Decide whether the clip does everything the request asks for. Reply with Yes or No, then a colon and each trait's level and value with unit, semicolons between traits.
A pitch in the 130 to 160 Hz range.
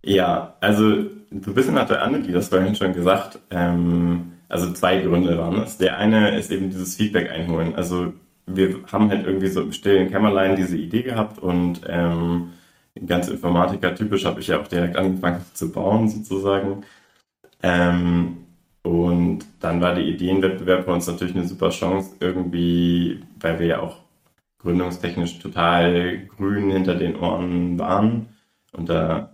No: very low, 90 Hz